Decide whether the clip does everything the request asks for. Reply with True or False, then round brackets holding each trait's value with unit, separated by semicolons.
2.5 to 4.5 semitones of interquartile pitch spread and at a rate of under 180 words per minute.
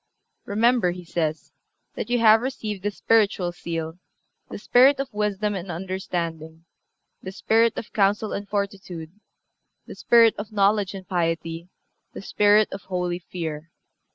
True (3.5 semitones; 140 wpm)